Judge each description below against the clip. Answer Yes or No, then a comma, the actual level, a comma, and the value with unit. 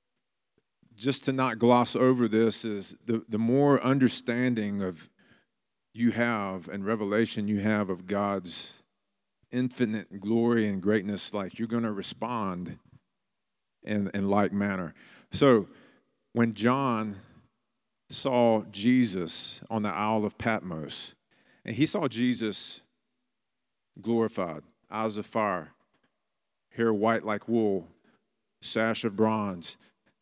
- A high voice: No, low, 110 Hz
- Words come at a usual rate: No, slow, 115 wpm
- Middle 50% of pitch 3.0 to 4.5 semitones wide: No, narrow, 2.5 semitones